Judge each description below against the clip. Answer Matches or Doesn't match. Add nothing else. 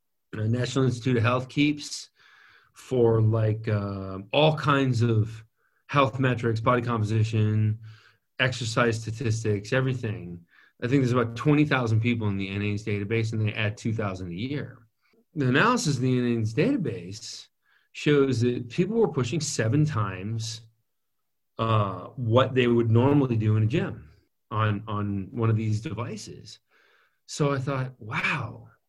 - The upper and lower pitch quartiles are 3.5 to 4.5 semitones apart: Doesn't match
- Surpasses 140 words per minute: Doesn't match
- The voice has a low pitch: Matches